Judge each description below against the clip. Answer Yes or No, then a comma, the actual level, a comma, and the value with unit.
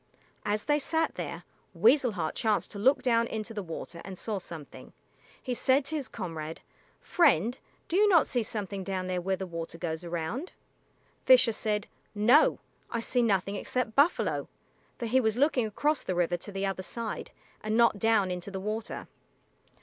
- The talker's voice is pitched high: Yes, high, 215 Hz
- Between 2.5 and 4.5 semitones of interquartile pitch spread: No, average, 5.1 semitones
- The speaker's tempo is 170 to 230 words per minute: Yes, average, 180 wpm